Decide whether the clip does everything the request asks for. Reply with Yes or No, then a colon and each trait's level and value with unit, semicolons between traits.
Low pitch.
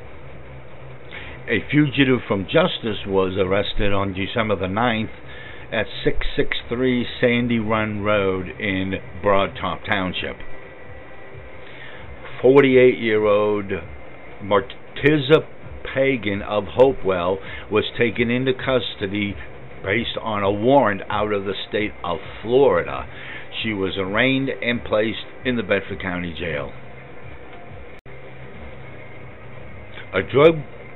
Yes: low, 105 Hz